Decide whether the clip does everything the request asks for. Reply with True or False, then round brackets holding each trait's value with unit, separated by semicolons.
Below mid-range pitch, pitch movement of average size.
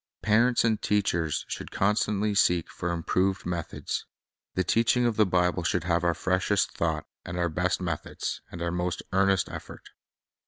True (90 Hz; 3.1 semitones)